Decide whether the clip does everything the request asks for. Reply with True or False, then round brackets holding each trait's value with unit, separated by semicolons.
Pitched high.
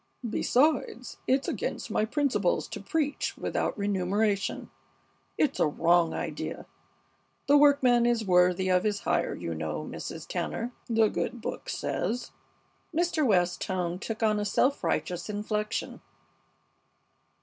True (210 Hz)